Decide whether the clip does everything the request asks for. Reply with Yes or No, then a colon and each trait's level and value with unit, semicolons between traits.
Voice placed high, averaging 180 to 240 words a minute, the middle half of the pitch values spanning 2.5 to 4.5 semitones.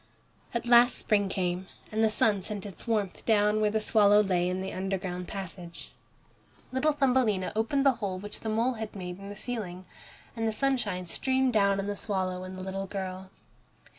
Yes: high, 205 Hz; average, 190 wpm; average, 3.1 semitones